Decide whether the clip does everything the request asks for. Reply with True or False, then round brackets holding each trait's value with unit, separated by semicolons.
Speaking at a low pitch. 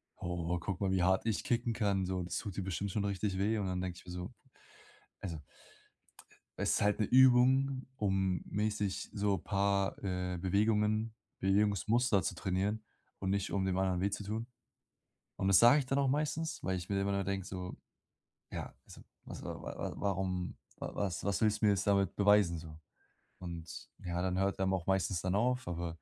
True (100 Hz)